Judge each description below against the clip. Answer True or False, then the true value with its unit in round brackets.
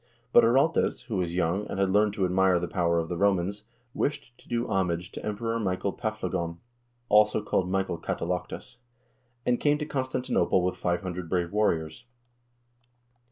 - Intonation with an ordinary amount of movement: True (3.5 semitones)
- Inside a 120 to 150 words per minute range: False (160 wpm)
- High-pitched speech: False (95 Hz)